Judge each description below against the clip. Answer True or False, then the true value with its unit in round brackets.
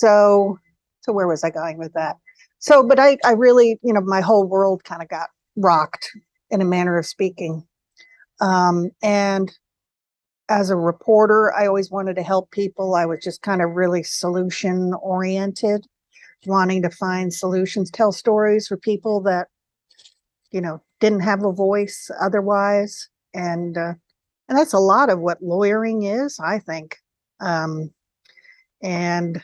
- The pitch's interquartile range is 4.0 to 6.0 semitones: False (3.0 semitones)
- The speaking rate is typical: True (155 wpm)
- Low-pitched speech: False (195 Hz)